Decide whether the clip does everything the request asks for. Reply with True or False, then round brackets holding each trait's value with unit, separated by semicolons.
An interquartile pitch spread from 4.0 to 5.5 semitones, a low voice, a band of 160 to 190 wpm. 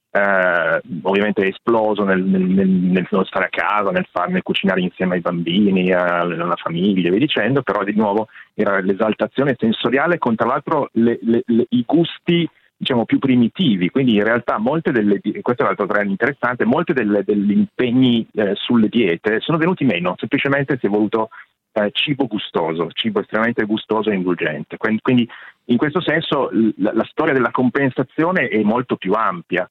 True (4.6 semitones; 110 Hz; 165 wpm)